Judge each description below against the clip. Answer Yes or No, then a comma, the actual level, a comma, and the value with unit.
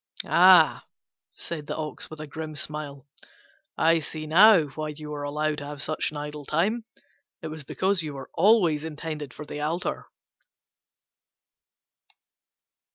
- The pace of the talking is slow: No, average, 145 wpm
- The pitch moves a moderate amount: No, narrow, 1.8 semitones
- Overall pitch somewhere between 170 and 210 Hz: No, medium, 155 Hz